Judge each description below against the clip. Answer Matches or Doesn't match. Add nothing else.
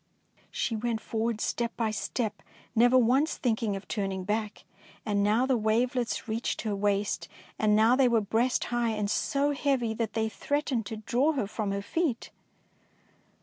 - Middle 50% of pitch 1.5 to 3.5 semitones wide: Matches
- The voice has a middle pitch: Doesn't match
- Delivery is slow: Doesn't match